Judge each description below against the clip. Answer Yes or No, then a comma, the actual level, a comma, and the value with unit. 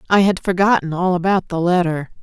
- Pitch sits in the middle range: Yes, medium, 180 Hz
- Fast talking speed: No, average, 190 wpm